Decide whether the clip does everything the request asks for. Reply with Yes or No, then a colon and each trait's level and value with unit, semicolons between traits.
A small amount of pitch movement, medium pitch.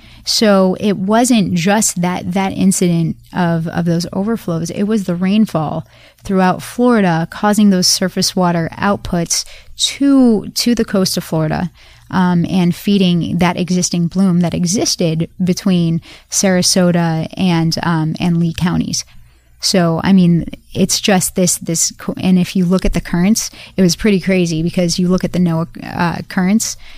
Yes: narrow, 2.3 semitones; medium, 180 Hz